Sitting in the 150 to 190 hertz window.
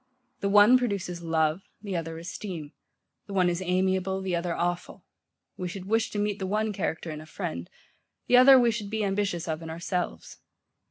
Yes: medium, 185 Hz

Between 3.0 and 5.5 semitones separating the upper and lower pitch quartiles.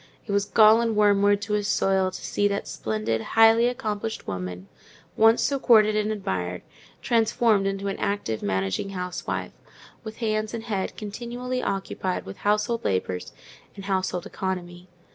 Yes: average, 3.4 semitones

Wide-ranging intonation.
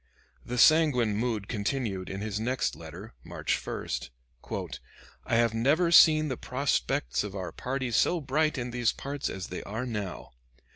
No: average, 5.0 semitones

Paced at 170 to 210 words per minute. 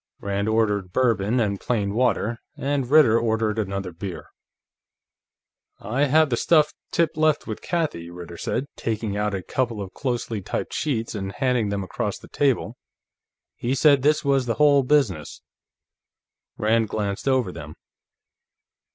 No: average, 145 wpm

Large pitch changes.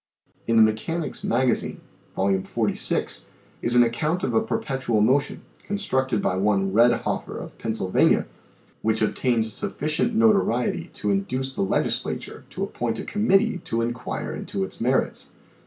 Yes: wide, 5.9 semitones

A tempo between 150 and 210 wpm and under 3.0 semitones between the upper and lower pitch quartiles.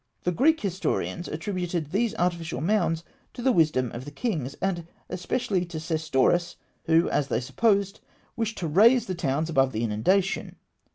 No: average, 160 wpm; average, 4.5 semitones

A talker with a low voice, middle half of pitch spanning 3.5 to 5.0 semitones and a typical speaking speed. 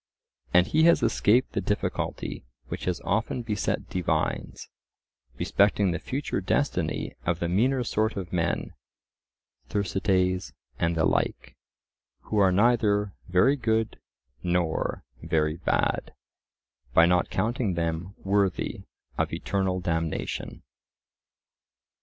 No: very low, 95 Hz; average, 3.9 semitones; slow, 110 wpm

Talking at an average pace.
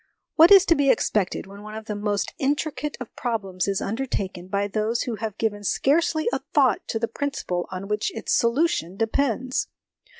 Yes: average, 190 wpm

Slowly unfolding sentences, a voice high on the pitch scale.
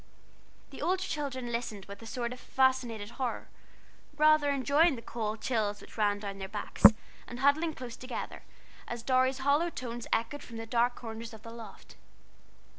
No: average, 170 wpm; high, 240 Hz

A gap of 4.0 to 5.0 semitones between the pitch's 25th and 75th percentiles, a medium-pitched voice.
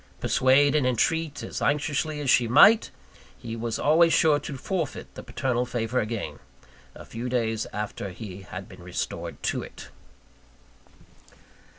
No: average, 4.5 semitones; low, 125 Hz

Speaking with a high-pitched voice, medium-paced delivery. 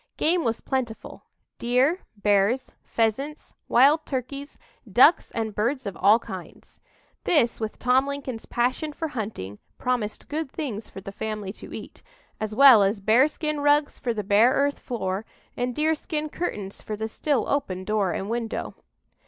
Yes: high, 240 Hz; average, 155 wpm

